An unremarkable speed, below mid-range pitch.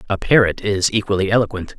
Yes: average, 170 wpm; low, 100 Hz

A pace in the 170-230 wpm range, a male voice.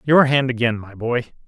Yes: fast, 205 wpm; male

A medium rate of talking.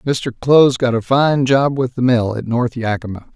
No: fast, 215 wpm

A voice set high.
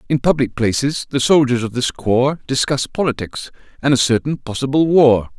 No: low, 130 Hz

